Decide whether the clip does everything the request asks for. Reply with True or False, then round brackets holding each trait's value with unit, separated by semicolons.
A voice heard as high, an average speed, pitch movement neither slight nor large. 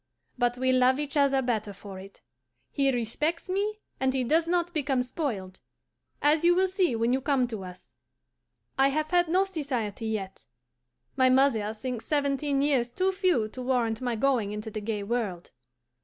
True (260 Hz; 175 wpm; 5.0 semitones)